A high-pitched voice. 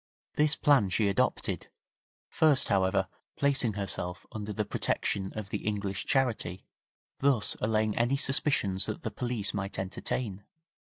No: low, 105 Hz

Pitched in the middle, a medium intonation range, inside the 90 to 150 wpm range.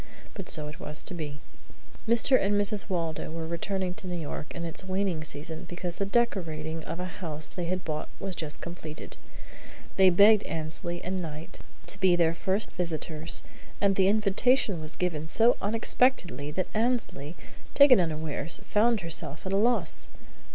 No: medium, 175 Hz; average, 3.8 semitones; average, 165 wpm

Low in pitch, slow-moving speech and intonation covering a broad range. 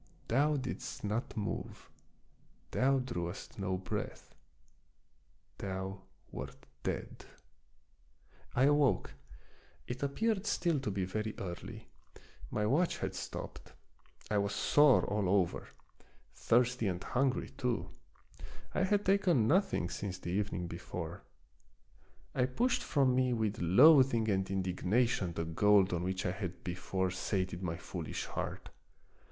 Yes: low, 105 Hz; slow, 125 wpm; wide, 6.1 semitones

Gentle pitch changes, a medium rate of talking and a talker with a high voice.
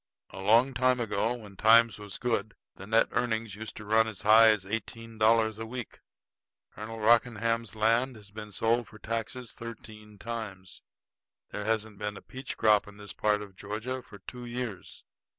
No: narrow, 1.9 semitones; average, 175 wpm; low, 110 Hz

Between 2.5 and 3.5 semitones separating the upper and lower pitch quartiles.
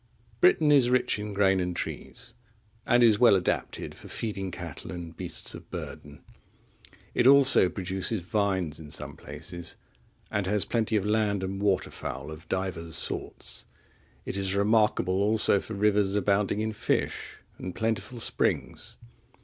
Yes: average, 2.9 semitones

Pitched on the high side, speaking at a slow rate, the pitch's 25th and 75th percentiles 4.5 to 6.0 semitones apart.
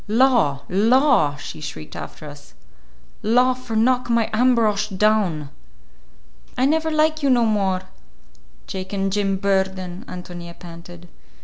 Yes: high, 205 Hz; slow, 125 wpm; wide, 5.6 semitones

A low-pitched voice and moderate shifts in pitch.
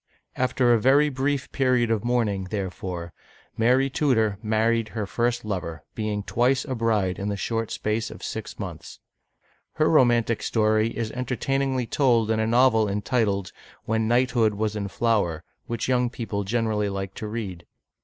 Yes: low, 115 Hz; average, 3.0 semitones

